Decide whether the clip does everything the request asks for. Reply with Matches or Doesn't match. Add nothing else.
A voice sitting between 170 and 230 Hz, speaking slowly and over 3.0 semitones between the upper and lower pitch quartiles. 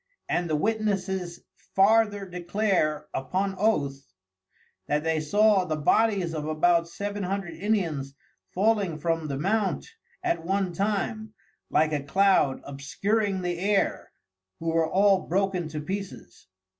Matches